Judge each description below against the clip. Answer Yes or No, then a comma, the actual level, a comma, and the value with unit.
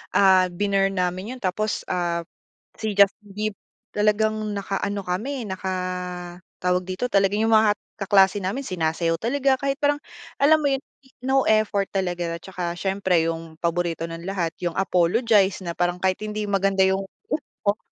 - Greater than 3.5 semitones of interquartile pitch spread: No, average, 3.0 semitones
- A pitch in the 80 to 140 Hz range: No, high, 195 Hz